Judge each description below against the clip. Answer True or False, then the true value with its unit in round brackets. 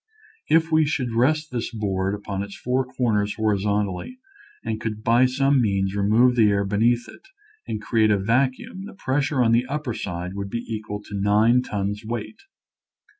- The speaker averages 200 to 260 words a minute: False (175 wpm)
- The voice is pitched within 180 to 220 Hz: False (115 Hz)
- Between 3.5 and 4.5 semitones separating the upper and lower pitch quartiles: True (3.8 semitones)